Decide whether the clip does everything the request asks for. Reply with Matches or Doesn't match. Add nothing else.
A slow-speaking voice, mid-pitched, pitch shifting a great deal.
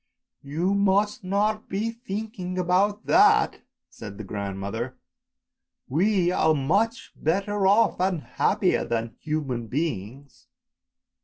Matches